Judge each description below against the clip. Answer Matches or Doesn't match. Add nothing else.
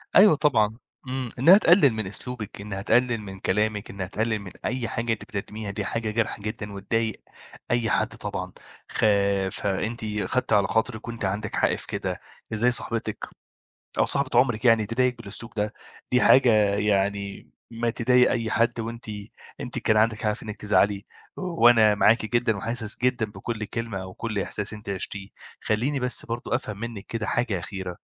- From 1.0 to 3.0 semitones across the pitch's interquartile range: Matches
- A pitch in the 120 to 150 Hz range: Doesn't match